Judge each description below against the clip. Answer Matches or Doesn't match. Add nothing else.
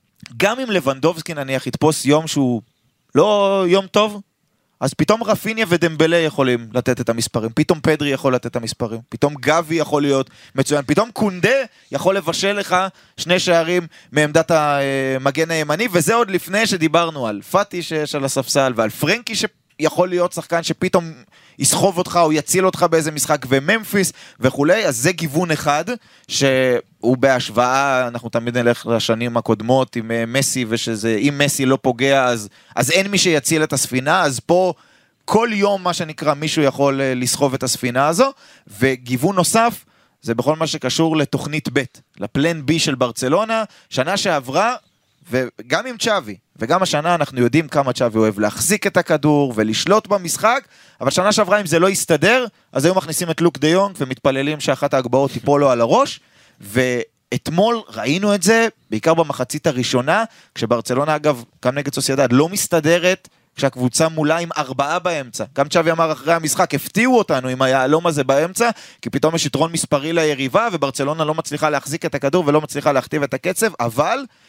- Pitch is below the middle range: Doesn't match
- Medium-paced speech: Doesn't match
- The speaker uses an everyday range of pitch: Matches